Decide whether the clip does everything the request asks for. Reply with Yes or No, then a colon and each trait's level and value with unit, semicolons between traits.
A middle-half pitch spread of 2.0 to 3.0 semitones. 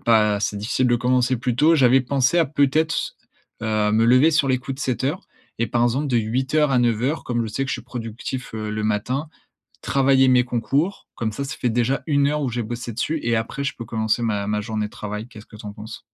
No: average, 3.6 semitones